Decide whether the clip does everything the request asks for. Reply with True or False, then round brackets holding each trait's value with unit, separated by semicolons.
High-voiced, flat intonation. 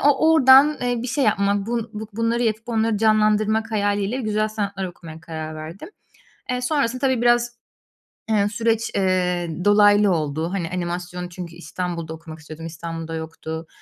False (205 Hz; 5.1 semitones)